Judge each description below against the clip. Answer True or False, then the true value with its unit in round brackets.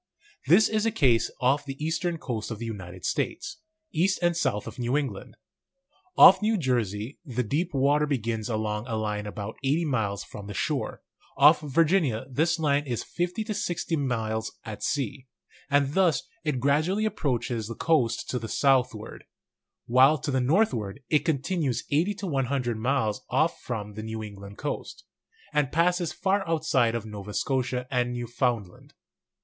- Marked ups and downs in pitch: True (6.0 semitones)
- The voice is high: False (130 Hz)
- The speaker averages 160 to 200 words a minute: True (165 wpm)